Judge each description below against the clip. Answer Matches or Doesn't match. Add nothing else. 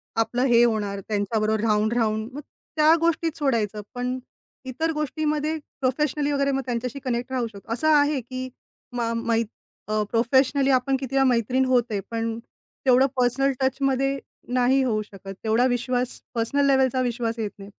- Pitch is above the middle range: Matches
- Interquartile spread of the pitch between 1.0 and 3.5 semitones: Matches